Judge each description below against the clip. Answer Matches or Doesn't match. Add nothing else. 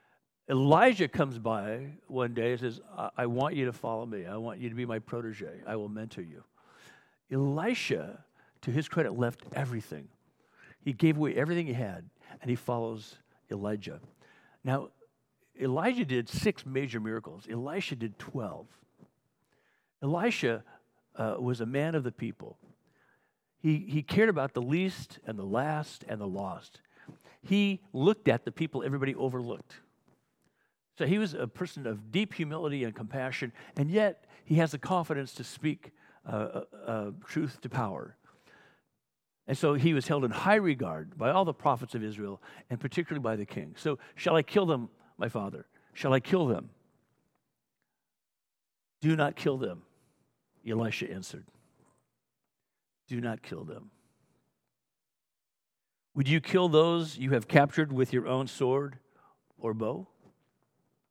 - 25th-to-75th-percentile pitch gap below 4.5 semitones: Doesn't match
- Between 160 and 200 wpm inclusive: Doesn't match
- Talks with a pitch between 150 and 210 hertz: Doesn't match